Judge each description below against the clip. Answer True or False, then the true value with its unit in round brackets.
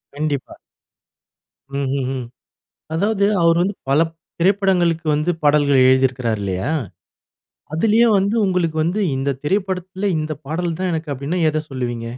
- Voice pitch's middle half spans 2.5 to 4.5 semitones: False (5.3 semitones)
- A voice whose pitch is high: False (160 Hz)